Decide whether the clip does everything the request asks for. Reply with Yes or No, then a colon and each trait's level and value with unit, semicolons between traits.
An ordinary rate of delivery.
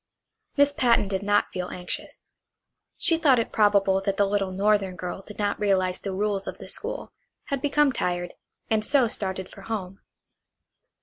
Yes: average, 170 wpm